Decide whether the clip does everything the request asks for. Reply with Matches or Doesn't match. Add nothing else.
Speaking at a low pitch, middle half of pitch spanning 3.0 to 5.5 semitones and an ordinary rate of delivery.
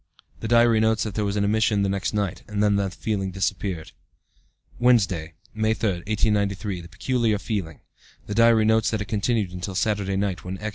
Doesn't match